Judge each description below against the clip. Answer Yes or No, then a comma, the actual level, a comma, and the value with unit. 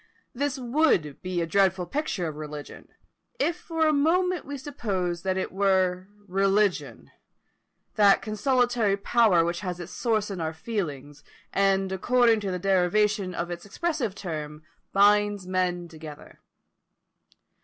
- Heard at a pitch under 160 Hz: No, high, 195 Hz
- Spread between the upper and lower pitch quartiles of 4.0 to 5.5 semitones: Yes, average, 4.6 semitones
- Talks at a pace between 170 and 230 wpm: No, slow, 135 wpm